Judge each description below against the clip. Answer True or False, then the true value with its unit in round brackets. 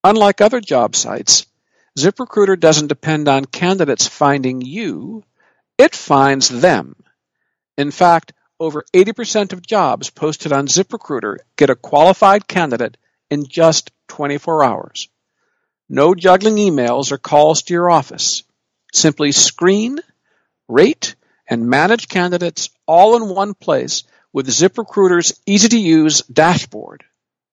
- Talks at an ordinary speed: False (120 wpm)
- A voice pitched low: False (175 Hz)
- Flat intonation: False (5.6 semitones)